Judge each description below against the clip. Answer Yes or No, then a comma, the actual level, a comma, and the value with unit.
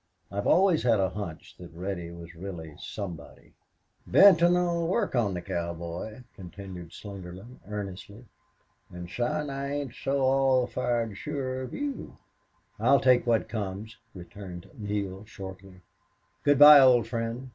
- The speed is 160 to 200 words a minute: No, slow, 135 wpm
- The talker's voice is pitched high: No, low, 105 Hz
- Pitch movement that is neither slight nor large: No, wide, 6.2 semitones